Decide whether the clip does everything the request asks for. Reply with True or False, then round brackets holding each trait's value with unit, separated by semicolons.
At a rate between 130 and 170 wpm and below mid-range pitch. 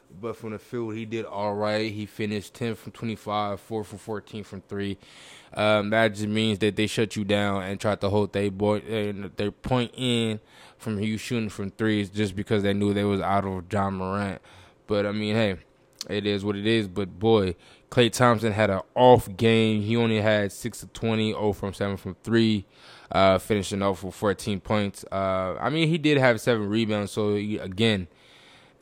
False (200 wpm; 105 Hz)